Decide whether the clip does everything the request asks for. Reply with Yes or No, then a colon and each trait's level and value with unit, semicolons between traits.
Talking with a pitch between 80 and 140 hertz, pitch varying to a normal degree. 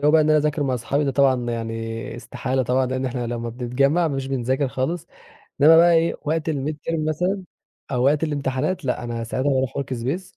Yes: low, 135 Hz; average, 3.6 semitones